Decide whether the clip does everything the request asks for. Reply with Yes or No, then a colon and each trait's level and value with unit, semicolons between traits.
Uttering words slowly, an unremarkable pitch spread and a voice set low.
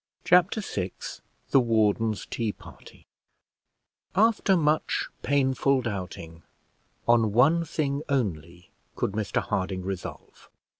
No: slow, 100 wpm; wide, 6.8 semitones; low, 115 Hz